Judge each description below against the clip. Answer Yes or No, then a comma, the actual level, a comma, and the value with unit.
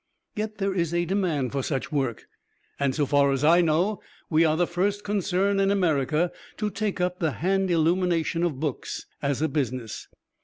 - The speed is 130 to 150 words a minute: No, average, 185 wpm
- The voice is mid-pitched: Yes, medium, 170 Hz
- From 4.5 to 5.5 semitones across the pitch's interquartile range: Yes, average, 4.8 semitones